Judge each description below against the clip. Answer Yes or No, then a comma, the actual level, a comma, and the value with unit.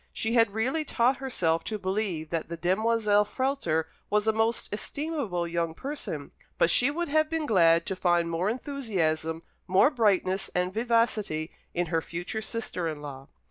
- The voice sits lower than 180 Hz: No, high, 205 Hz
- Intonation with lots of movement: Yes, wide, 5.8 semitones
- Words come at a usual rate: Yes, average, 165 wpm